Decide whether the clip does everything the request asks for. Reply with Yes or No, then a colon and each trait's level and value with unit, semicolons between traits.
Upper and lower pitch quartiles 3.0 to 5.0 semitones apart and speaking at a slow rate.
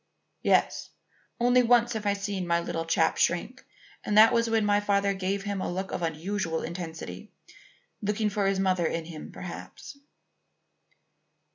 No: average, 3.5 semitones; average, 155 wpm